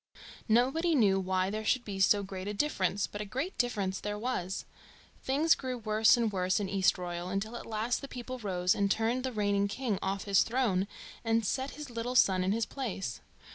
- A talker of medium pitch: No, high, 210 Hz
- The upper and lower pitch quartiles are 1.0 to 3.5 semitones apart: No, average, 4.2 semitones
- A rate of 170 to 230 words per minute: Yes, average, 200 wpm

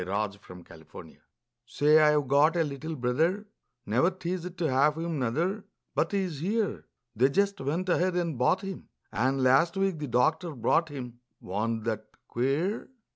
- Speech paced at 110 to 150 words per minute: No, average, 160 wpm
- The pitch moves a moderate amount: No, wide, 6.0 semitones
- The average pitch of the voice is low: No, medium, 150 Hz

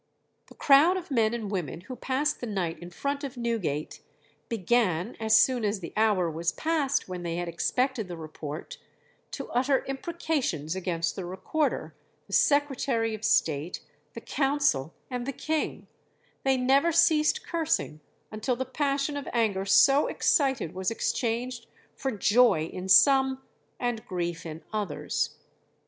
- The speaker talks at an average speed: Yes, average, 150 wpm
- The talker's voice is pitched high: Yes, high, 230 Hz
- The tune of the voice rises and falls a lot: Yes, wide, 7.2 semitones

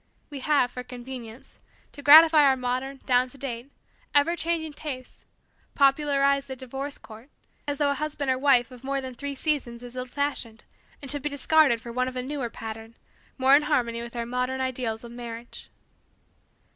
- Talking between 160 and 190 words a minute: Yes, average, 185 wpm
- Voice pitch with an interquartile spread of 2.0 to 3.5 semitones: Yes, average, 2.7 semitones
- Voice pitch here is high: Yes, very high, 260 Hz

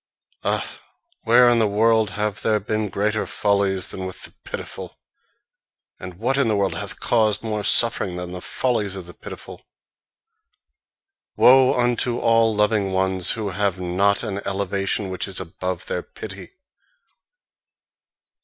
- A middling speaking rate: Yes, average, 145 wpm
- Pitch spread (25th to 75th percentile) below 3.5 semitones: Yes, average, 2.9 semitones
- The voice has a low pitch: Yes, low, 100 Hz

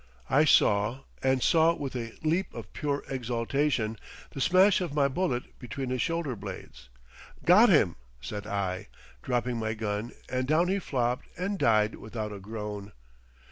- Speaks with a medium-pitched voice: No, low, 125 Hz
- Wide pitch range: Yes, wide, 5.9 semitones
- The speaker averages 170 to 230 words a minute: No, average, 155 wpm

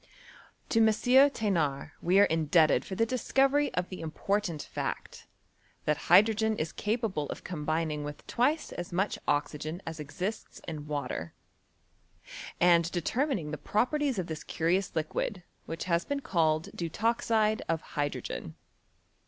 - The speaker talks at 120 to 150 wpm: Yes, slow, 135 wpm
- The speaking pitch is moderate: Yes, medium, 175 Hz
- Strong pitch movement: Yes, wide, 5.9 semitones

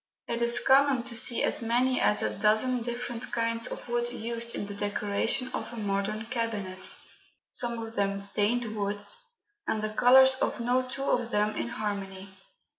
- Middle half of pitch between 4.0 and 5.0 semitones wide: No, average, 2.7 semitones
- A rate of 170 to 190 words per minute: Yes, average, 175 wpm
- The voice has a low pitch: No, high, 230 Hz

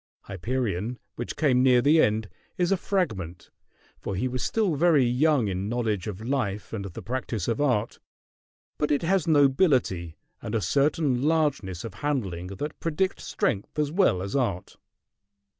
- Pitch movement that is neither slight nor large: No, wide, 6.6 semitones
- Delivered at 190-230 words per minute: No, average, 160 wpm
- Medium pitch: No, low, 125 Hz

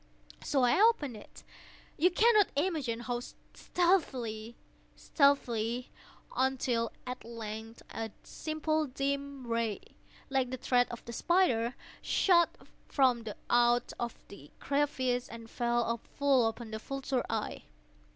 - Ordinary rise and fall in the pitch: Yes, average, 3.5 semitones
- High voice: Yes, very high, 250 Hz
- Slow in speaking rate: Yes, slow, 110 wpm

